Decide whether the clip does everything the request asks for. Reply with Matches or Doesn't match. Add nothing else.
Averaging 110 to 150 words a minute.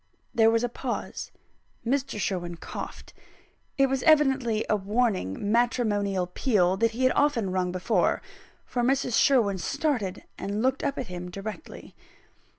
Matches